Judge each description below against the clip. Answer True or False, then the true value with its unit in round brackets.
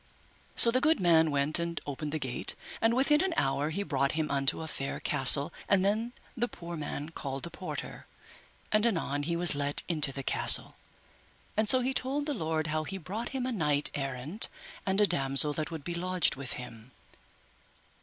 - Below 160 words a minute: False (195 wpm)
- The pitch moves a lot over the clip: True (6.6 semitones)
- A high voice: False (160 Hz)